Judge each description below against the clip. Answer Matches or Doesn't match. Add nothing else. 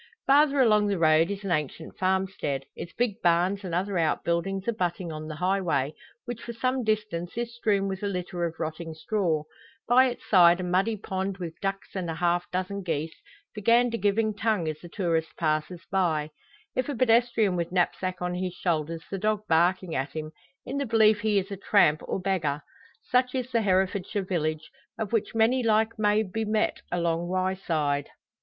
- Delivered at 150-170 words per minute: Doesn't match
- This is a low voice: Doesn't match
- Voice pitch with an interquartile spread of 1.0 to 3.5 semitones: Doesn't match